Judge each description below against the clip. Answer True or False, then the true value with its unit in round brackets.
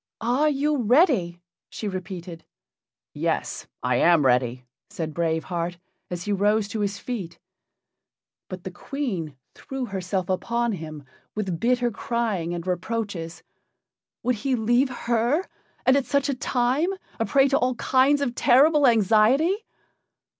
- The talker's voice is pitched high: True (220 Hz)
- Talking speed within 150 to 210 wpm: False (140 wpm)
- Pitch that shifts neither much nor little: False (6.5 semitones)